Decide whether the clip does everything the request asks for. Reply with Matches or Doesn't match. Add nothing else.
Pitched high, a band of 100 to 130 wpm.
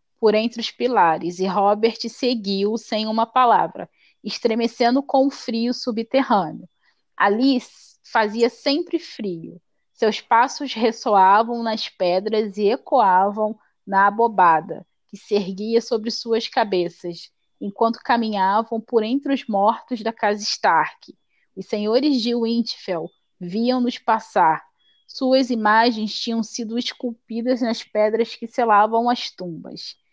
Matches